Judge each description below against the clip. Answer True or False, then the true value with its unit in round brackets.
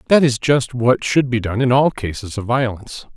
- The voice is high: False (125 Hz)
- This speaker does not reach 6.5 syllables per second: True (5.2 syllables/s)